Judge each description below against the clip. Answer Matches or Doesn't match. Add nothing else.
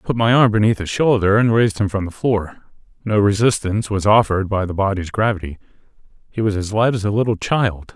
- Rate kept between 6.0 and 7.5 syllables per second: Matches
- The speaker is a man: Matches